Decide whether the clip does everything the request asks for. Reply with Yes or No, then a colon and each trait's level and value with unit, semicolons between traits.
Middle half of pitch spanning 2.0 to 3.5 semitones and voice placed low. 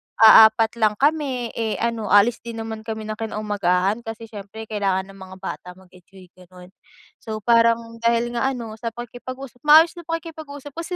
No: average, 2.7 semitones; high, 225 Hz